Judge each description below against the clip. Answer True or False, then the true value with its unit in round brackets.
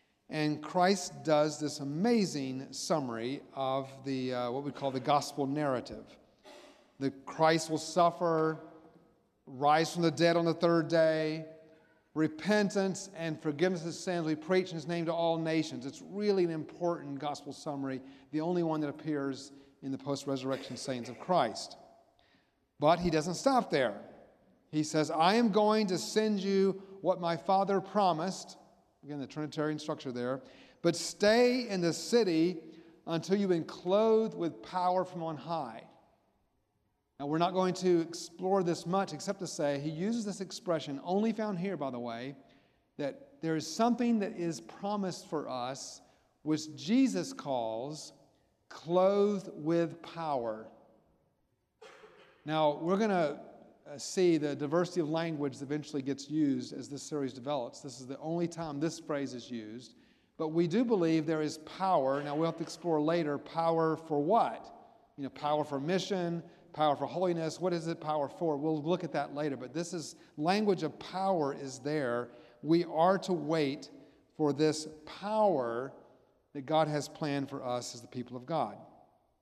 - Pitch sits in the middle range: True (160 Hz)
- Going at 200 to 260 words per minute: False (160 wpm)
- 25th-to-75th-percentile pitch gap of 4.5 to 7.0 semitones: False (3.8 semitones)